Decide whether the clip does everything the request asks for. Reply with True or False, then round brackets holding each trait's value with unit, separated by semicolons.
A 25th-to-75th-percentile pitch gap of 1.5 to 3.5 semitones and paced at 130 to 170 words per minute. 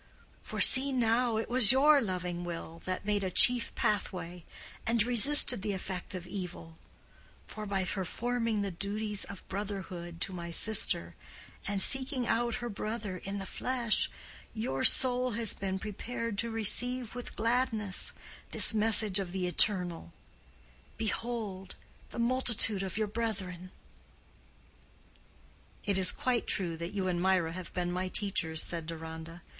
False (4.3 semitones; 145 wpm)